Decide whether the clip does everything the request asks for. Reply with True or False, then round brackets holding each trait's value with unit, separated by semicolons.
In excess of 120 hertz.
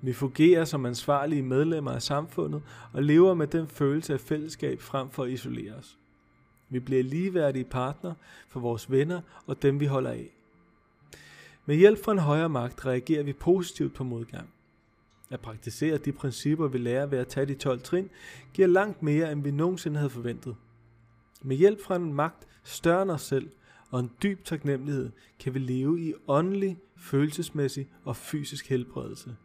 True (140 Hz)